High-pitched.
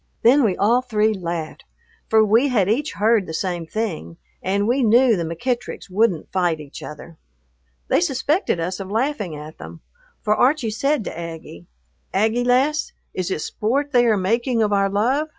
Yes: high, 215 Hz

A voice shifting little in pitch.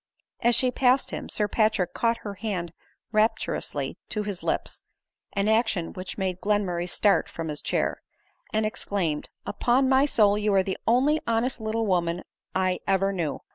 No: average, 3.6 semitones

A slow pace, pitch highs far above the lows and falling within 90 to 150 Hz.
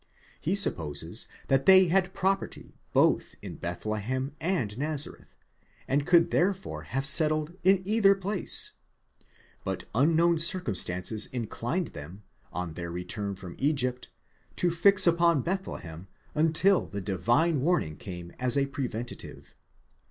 Yes: slow, 120 wpm; wide, 9.0 semitones; medium, 140 Hz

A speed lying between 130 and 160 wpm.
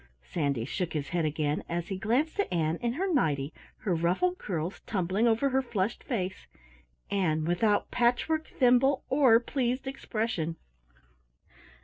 Yes: average, 140 wpm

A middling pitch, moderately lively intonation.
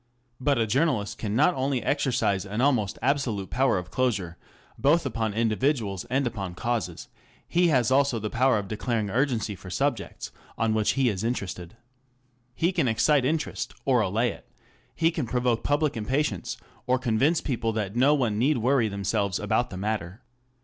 No: low, 120 Hz; average, 4.6 semitones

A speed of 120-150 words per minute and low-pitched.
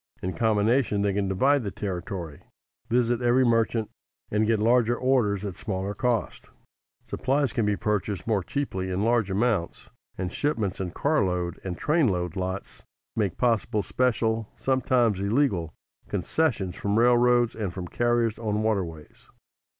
Yes: average, 145 wpm; low, 110 Hz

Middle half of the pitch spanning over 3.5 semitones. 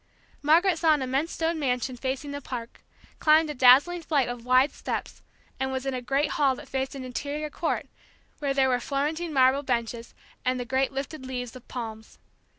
No: average, 2.8 semitones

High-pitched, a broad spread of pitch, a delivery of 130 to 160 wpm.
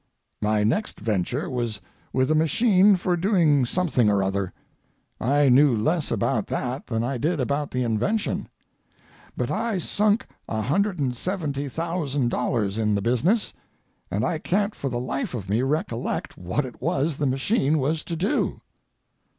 No: medium, 140 Hz; wide, 6.5 semitones; average, 145 wpm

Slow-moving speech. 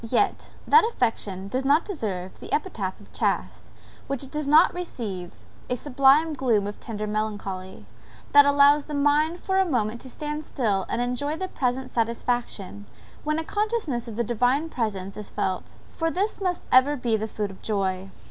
No: average, 175 wpm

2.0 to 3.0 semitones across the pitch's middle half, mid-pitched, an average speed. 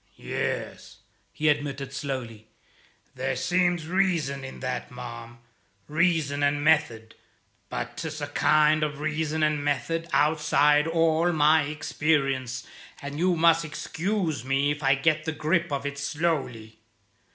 No: narrow, 2.6 semitones; medium, 150 Hz; slow, 130 wpm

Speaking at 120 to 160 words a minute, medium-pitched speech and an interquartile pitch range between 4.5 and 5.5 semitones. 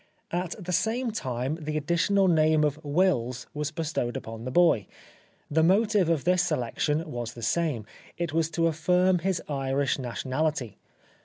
Yes: average, 155 wpm; medium, 155 Hz; average, 4.8 semitones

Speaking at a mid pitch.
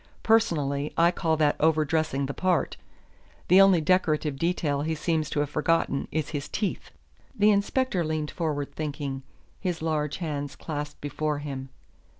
Yes: medium, 155 Hz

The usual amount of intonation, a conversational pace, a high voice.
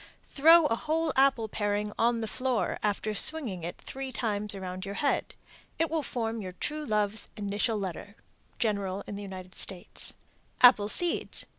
Yes: average, 4.6 semitones; average, 160 wpm; high, 215 Hz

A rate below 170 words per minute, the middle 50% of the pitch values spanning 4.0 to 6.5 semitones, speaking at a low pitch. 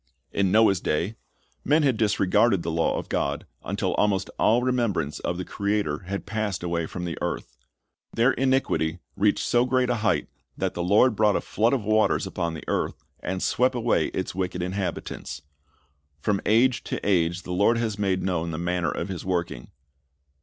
No: average, 180 wpm; average, 4.3 semitones; low, 100 Hz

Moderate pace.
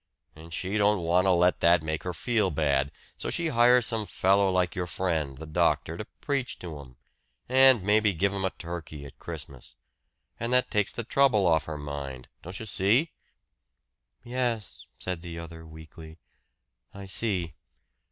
Yes: average, 170 wpm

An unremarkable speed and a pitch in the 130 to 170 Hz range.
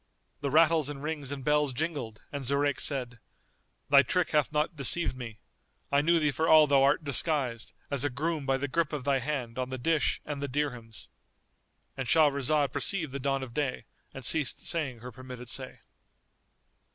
Yes: average, 185 wpm; medium, 140 Hz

